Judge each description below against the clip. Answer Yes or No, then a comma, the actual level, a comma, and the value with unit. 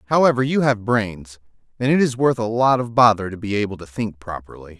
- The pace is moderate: No, fast, 225 wpm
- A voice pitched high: No, low, 110 Hz